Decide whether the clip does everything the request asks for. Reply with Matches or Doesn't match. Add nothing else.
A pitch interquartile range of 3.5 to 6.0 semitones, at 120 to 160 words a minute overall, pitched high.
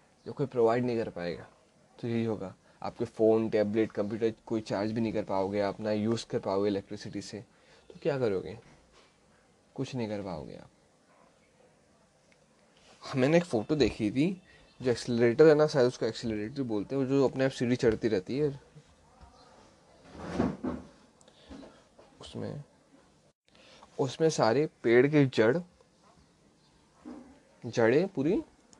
Doesn't match